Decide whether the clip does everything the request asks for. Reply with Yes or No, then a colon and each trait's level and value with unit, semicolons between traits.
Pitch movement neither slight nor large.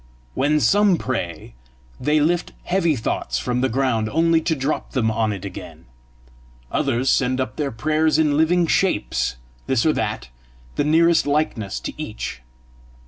No: wide, 5.9 semitones